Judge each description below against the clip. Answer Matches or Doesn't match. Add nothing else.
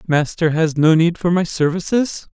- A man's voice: Matches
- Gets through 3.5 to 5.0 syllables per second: Matches